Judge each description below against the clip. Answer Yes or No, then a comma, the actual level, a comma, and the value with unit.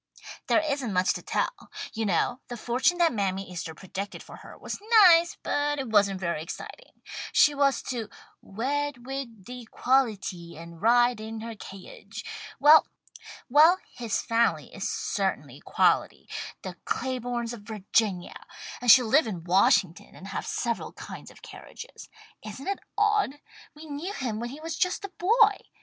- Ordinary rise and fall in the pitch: No, wide, 6.3 semitones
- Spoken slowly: No, average, 155 wpm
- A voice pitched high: Yes, high, 240 Hz